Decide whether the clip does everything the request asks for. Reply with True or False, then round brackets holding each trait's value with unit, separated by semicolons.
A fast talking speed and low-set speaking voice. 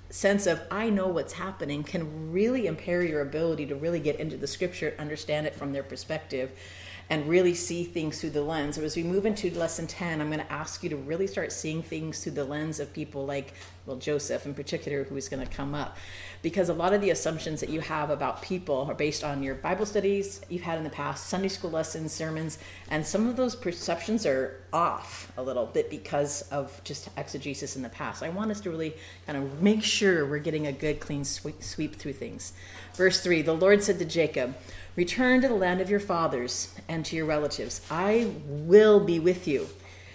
False (215 wpm; 160 Hz)